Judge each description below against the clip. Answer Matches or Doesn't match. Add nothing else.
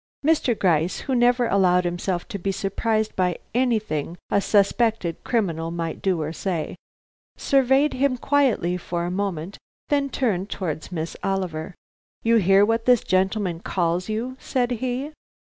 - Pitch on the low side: Doesn't match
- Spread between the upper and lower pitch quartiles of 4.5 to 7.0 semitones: Matches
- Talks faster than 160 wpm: Doesn't match